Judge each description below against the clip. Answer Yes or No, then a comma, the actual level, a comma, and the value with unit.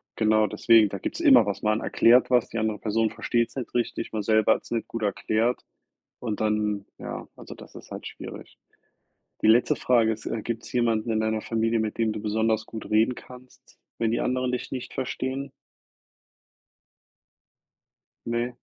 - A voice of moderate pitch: No, low, 115 Hz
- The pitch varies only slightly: Yes, narrow, 1.9 semitones